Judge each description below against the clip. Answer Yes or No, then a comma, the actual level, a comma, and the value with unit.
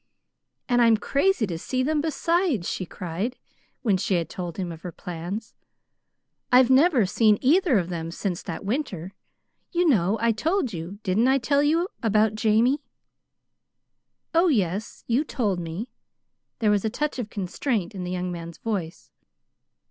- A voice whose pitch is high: Yes, high, 215 Hz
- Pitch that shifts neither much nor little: No, wide, 6.5 semitones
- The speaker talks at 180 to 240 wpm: No, average, 160 wpm